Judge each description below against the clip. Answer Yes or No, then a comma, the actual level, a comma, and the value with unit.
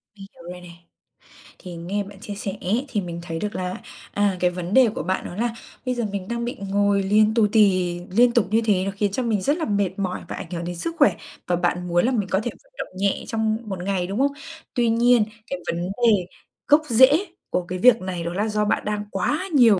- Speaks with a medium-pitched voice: No, high, 205 Hz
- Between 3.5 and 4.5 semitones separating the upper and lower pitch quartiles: Yes, average, 4.2 semitones